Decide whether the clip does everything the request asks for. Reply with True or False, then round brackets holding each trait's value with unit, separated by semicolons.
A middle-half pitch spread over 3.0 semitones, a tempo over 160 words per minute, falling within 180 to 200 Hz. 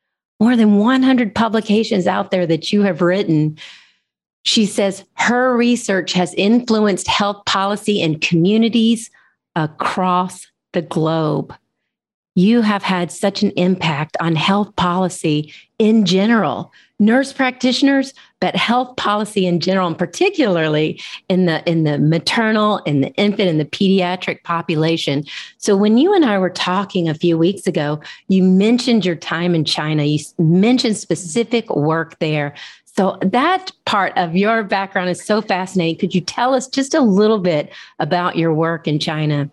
False (4.8 semitones; 155 wpm; 190 Hz)